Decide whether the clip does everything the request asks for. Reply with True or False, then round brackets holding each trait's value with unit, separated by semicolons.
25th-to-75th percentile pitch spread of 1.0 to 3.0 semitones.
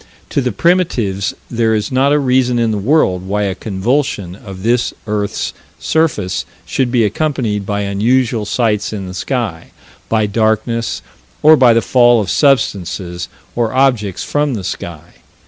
False (4.4 semitones)